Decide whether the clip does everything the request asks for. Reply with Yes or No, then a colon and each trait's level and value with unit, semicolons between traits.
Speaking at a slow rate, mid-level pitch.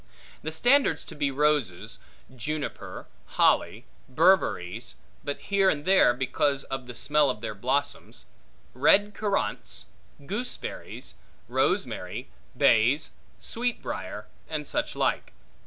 Yes: slow, 105 wpm; medium, 145 Hz